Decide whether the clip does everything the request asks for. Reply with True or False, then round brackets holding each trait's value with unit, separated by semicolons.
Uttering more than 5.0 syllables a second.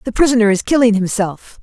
True (6.0 syllables/s)